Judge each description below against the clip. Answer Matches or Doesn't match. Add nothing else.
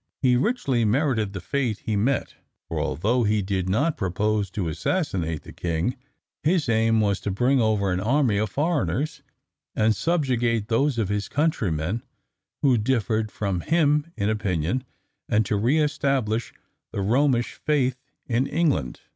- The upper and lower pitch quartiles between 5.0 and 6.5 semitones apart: Matches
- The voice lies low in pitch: Matches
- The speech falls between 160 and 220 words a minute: Doesn't match